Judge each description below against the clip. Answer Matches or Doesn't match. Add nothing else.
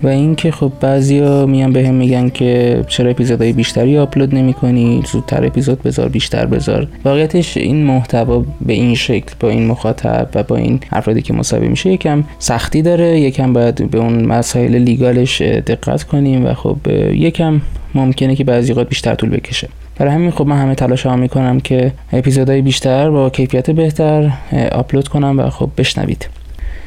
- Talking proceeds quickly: Matches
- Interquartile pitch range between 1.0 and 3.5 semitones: Matches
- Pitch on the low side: Matches